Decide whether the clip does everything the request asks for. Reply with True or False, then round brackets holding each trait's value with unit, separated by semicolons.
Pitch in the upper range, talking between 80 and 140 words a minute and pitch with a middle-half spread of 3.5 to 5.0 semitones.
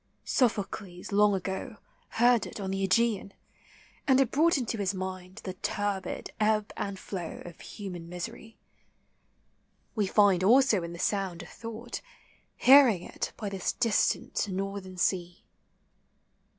False (200 Hz; 135 wpm; 3.0 semitones)